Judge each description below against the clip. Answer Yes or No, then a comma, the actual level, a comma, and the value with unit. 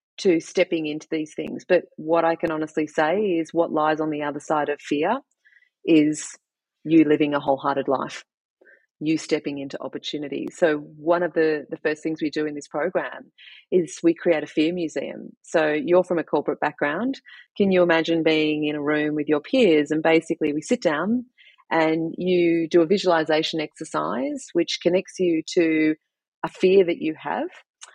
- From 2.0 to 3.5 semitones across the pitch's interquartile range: Yes, narrow, 2.4 semitones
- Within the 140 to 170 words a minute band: No, average, 180 wpm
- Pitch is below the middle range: No, medium, 160 Hz